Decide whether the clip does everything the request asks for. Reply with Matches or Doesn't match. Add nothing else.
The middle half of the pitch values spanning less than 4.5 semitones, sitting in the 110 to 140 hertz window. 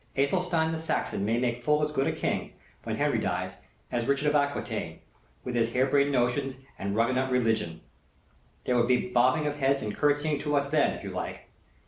Matches